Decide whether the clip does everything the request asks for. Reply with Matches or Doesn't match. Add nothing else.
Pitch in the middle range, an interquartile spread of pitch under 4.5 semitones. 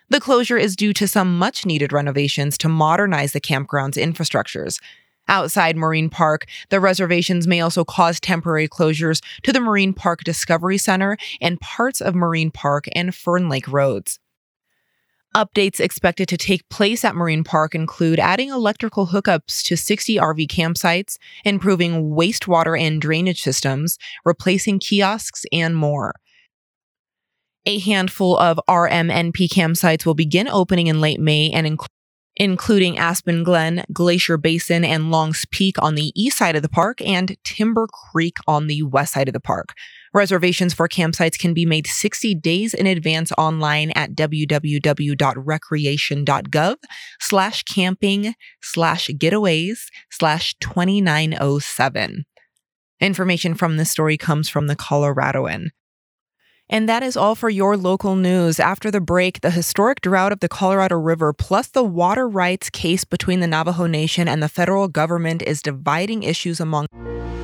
Matches